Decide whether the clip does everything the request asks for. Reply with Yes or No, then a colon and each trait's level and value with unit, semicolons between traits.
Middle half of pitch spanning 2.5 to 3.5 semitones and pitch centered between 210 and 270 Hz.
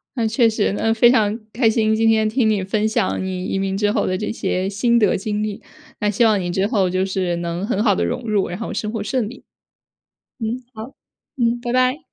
Yes: average, 2.8 semitones; high, 215 Hz